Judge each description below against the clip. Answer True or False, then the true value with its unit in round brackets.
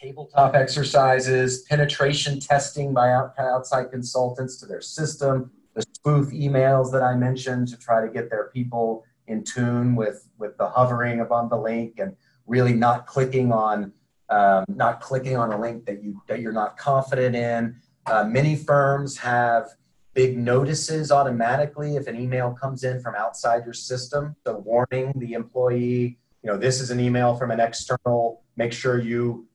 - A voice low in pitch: True (125 Hz)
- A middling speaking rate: True (165 wpm)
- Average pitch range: False (2.2 semitones)